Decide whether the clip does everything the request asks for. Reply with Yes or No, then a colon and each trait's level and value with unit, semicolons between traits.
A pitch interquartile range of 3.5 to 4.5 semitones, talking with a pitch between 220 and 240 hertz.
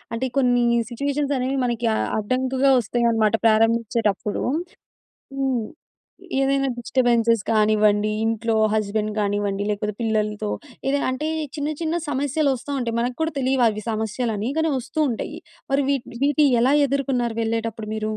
Yes: average, 3.8 semitones; high, 235 Hz